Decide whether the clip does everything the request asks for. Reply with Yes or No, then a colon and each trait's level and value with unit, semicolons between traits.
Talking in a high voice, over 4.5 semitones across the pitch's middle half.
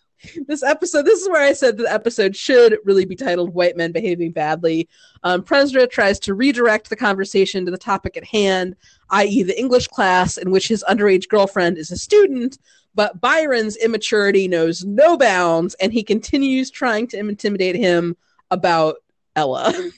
Yes: high, 205 Hz; wide, 5.4 semitones